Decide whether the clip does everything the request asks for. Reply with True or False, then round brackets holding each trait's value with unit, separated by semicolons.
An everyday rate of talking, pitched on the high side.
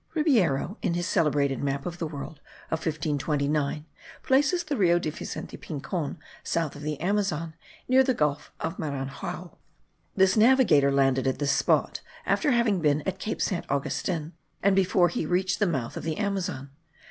False (165 wpm; 165 Hz)